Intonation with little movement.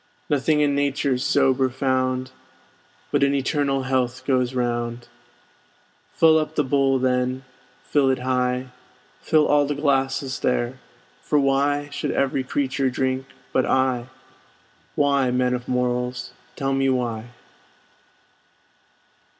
Yes: narrow, 1.8 semitones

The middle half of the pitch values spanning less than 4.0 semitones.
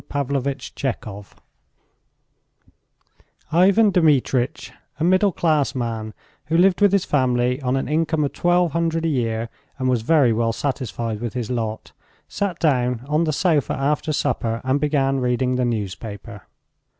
No: average, 5.1 semitones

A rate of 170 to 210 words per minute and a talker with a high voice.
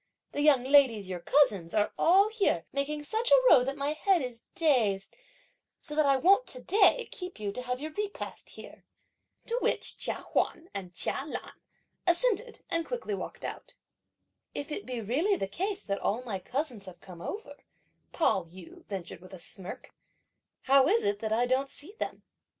Yes: average, 185 wpm; very high, 280 Hz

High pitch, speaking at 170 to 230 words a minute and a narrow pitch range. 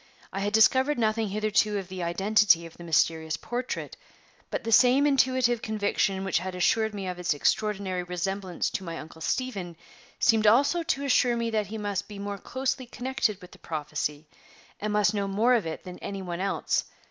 No: high, 205 Hz; average, 190 wpm; average, 4.3 semitones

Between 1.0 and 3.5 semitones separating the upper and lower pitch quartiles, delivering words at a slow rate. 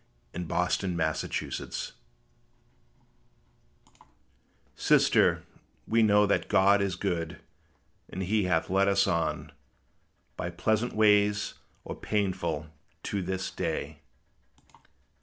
Yes: average, 2.9 semitones; slow, 105 wpm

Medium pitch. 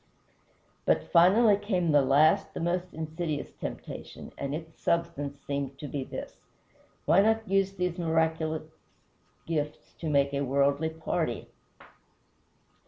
Yes: medium, 160 Hz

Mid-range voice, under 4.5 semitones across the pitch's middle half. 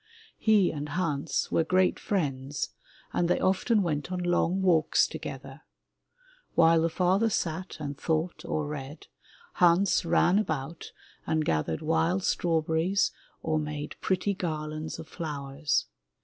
Yes: medium, 165 Hz; average, 3.3 semitones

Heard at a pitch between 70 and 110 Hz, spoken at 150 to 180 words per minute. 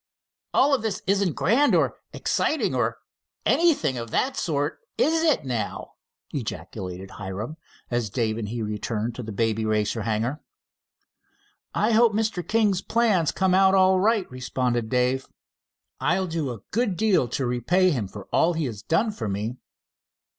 No: medium, 140 Hz; average, 155 wpm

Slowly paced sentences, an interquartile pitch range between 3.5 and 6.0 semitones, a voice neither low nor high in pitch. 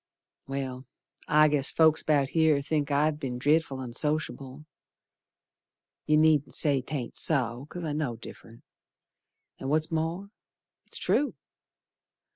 No: slow, 120 wpm; average, 2.7 semitones; medium, 150 Hz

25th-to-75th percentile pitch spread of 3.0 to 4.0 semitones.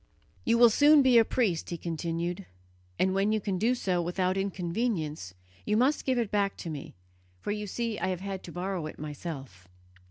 No: average, 4.6 semitones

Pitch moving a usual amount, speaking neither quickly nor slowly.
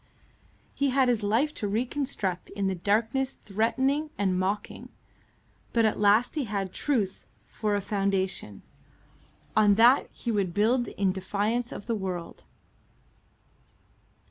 No: average, 3.7 semitones; slow, 130 wpm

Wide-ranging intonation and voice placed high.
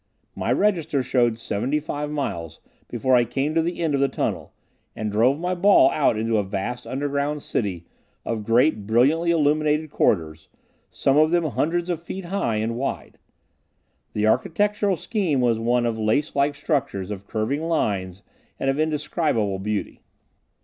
No: wide, 6.0 semitones; low, 135 Hz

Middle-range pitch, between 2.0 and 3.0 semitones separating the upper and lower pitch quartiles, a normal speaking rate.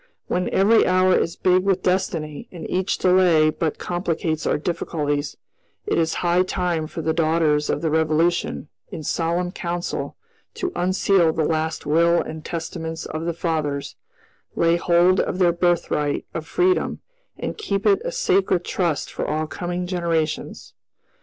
Yes: medium, 170 Hz; narrow, 2.4 semitones; average, 155 wpm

